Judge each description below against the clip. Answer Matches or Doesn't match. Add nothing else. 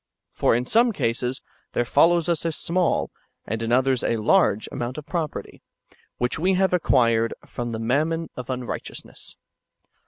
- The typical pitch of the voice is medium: Doesn't match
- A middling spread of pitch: Doesn't match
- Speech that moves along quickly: Doesn't match